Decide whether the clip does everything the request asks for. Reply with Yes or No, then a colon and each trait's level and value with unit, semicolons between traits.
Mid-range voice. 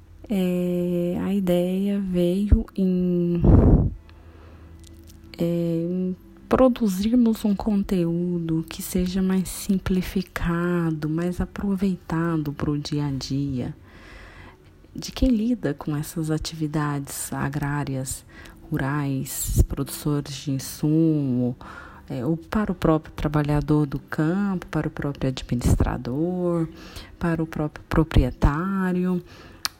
Yes: medium, 160 Hz